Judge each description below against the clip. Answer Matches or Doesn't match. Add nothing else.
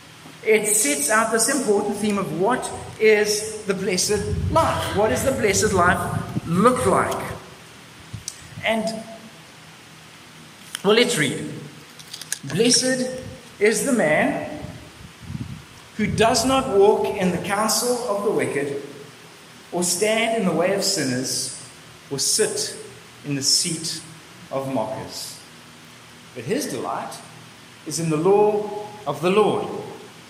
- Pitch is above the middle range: Matches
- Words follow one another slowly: Matches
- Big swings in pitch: Matches